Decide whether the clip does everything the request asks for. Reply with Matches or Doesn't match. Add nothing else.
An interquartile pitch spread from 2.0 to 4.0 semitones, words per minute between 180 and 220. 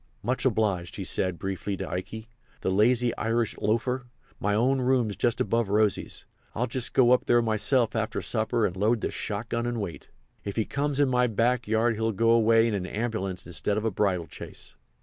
Matches